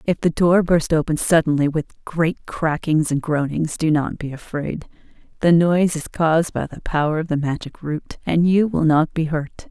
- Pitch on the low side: No, medium, 160 Hz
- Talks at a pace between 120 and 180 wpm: No, average, 200 wpm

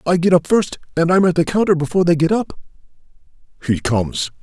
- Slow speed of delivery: No, fast, 205 wpm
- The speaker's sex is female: No, male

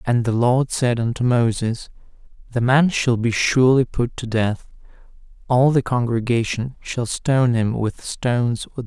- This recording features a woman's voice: No, male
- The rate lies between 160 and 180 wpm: Yes, average, 170 wpm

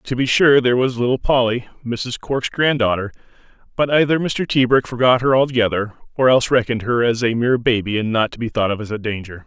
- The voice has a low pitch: Yes, low, 120 Hz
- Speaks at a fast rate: Yes, fast, 215 wpm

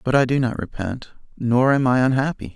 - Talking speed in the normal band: No, fast, 210 wpm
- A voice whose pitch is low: Yes, low, 125 Hz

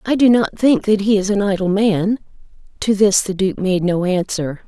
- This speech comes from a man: No, female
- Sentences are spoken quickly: Yes, fast, 220 wpm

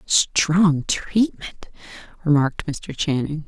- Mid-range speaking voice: Yes, medium, 160 Hz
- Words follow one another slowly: Yes, slow, 85 wpm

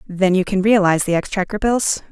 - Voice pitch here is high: Yes, high, 195 Hz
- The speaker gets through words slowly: No, average, 200 wpm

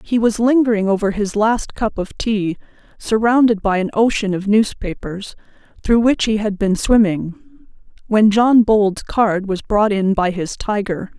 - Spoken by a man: No, female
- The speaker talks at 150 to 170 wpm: Yes, average, 165 wpm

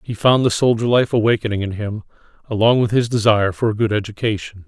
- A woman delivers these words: No, male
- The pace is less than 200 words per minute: No, fast, 205 wpm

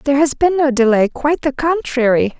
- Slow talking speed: No, average, 200 wpm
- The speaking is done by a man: No, female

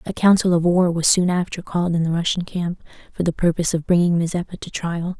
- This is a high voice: No, medium, 175 Hz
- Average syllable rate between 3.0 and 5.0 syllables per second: No, 6.1 syllables/s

